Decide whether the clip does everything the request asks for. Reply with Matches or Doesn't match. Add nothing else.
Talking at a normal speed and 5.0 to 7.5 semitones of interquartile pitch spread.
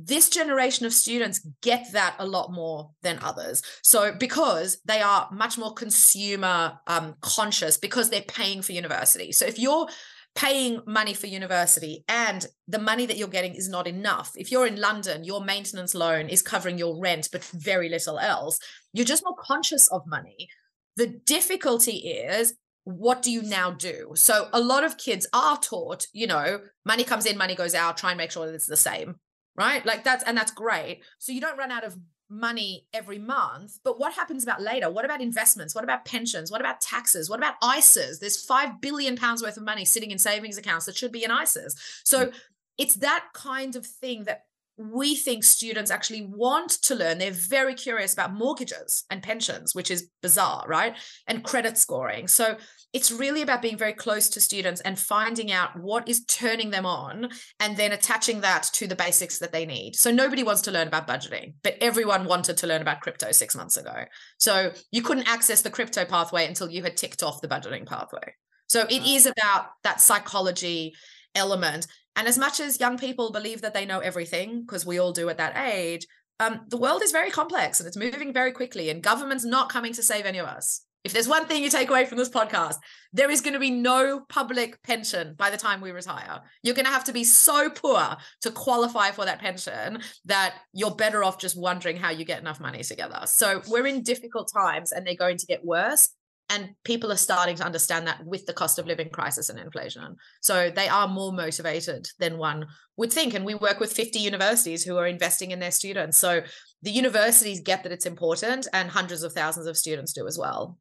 Doesn't match